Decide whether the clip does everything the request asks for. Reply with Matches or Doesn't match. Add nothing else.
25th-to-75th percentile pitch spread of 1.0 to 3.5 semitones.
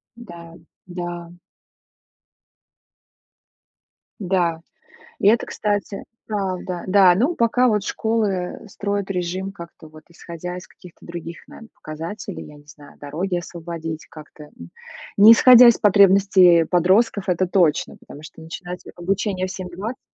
Matches